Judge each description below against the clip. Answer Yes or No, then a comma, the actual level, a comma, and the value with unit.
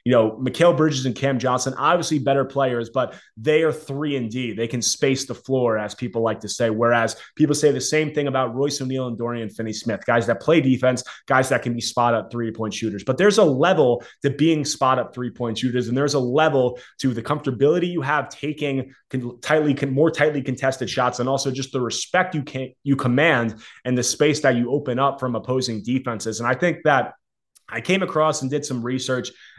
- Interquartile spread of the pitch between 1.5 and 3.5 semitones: Yes, average, 3.2 semitones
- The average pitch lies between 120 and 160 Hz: Yes, low, 130 Hz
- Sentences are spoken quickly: Yes, fast, 220 wpm